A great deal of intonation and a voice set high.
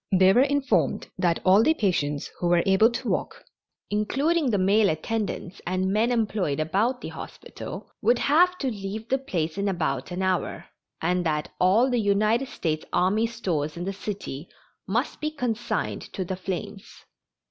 No: average, 4.6 semitones; high, 200 Hz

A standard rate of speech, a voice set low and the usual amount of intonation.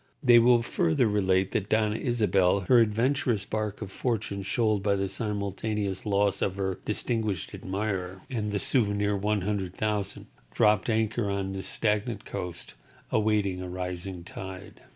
No: average, 145 wpm; low, 105 Hz; narrow, 2.3 semitones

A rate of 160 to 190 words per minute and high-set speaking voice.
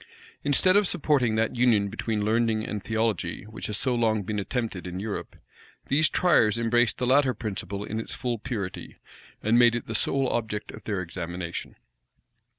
No: average, 170 wpm; low, 110 Hz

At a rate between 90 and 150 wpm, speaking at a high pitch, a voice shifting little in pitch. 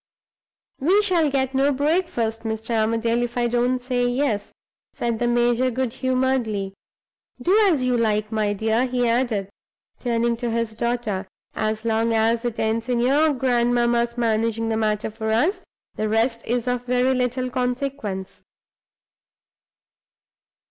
Yes: average, 140 wpm; high, 240 Hz; narrow, 2.3 semitones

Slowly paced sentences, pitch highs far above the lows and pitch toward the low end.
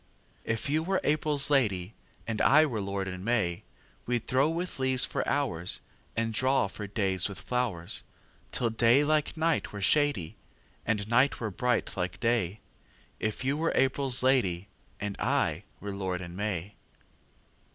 Yes: slow, 130 wpm; wide, 5.7 semitones; low, 115 Hz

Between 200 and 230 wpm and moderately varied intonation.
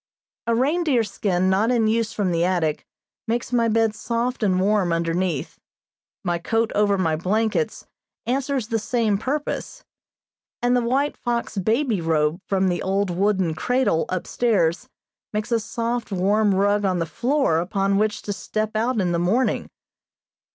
No: average, 155 wpm; average, 4.2 semitones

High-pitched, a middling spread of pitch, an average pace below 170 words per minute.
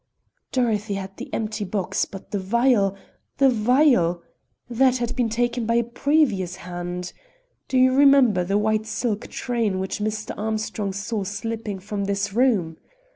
Yes: high, 215 Hz; average, 3.6 semitones; average, 150 wpm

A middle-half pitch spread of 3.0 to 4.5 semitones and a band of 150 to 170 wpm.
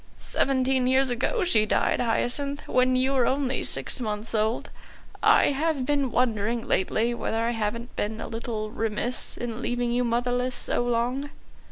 No: narrow, 2.4 semitones; average, 160 wpm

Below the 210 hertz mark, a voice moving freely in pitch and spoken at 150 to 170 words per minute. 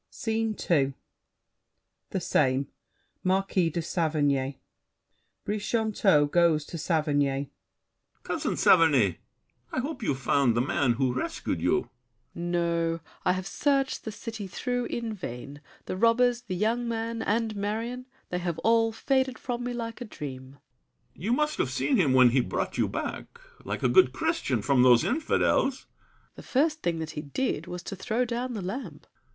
Yes: high, 190 Hz; wide, 8.3 semitones; average, 160 wpm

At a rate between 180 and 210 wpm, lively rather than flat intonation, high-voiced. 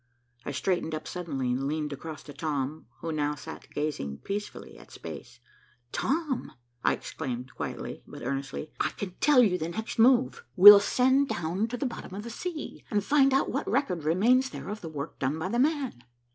No: average, 190 wpm; wide, 8.7 semitones; medium, 180 Hz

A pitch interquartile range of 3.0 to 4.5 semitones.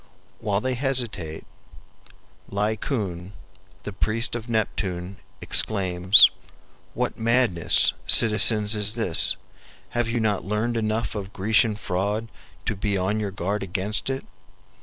No: narrow, 2.6 semitones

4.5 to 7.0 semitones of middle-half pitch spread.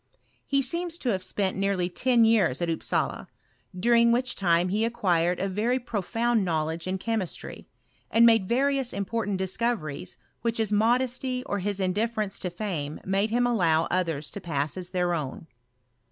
Yes: average, 4.8 semitones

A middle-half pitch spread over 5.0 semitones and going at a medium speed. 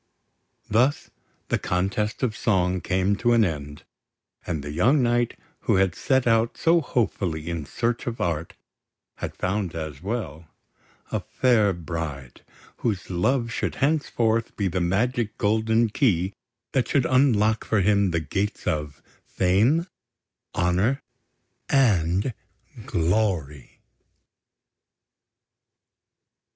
No: wide, 5.4 semitones; slow, 115 wpm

